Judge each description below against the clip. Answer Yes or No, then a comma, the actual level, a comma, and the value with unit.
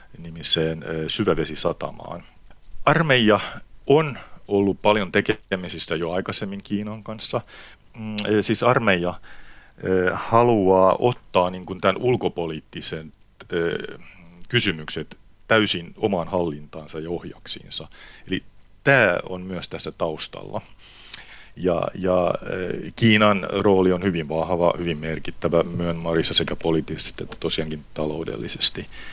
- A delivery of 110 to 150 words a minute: No, slow, 95 wpm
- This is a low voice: Yes, very low, 90 Hz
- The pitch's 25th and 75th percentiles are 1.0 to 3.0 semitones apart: No, average, 3.6 semitones